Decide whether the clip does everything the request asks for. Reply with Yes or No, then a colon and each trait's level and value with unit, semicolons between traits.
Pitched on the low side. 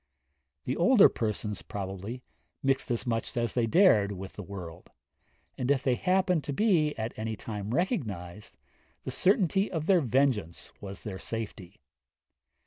Yes: low, 115 Hz